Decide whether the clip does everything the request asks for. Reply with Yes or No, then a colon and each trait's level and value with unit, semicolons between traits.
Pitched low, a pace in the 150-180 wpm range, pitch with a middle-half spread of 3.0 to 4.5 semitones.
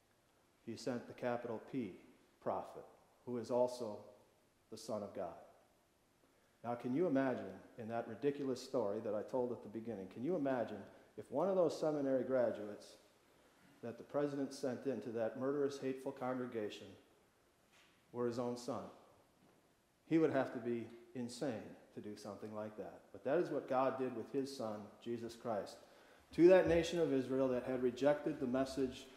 No: low, 125 Hz; average, 165 wpm; narrow, 2.5 semitones